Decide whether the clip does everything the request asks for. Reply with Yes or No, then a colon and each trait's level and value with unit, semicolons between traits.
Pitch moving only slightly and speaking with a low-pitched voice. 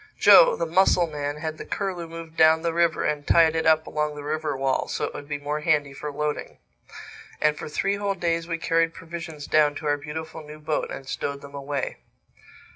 No: narrow, 2.1 semitones; medium, 155 Hz